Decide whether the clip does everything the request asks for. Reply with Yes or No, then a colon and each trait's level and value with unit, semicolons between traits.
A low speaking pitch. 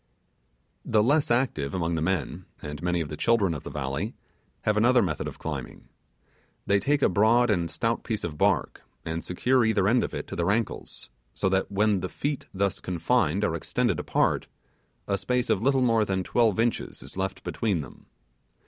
Yes: low, 100 Hz